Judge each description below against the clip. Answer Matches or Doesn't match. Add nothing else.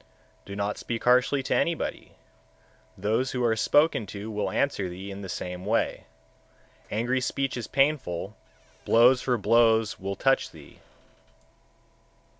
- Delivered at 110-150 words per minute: Matches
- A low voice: Matches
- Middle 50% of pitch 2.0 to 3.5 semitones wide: Doesn't match